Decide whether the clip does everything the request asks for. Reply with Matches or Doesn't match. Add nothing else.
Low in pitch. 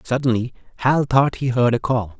Matches